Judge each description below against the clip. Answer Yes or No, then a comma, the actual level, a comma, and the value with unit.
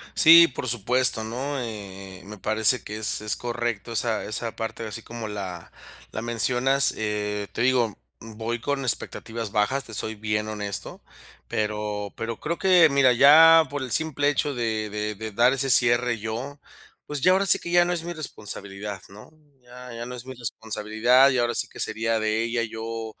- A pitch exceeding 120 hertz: No, low, 115 Hz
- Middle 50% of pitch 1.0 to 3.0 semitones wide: No, average, 3.4 semitones